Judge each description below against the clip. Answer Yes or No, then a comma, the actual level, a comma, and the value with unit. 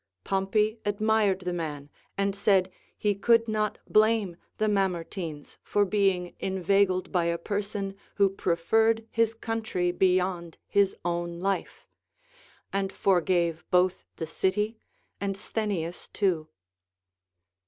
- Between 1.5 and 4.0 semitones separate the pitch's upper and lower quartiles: Yes, average, 2.9 semitones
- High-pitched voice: Yes, high, 195 Hz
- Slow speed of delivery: Yes, slow, 115 wpm